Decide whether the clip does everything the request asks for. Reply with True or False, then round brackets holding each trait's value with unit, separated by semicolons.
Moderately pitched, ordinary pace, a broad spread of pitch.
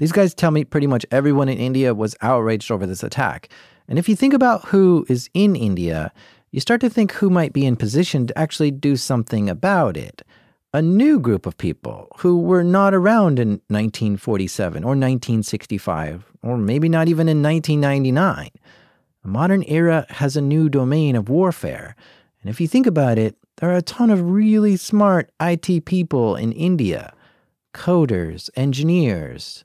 True (150 Hz; 170 wpm; 7.2 semitones)